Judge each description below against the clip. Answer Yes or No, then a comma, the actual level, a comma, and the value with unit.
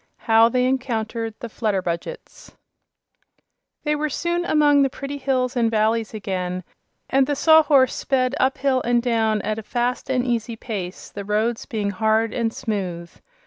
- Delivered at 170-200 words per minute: No, average, 155 wpm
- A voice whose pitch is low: No, high, 235 Hz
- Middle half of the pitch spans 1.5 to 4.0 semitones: Yes, average, 3.5 semitones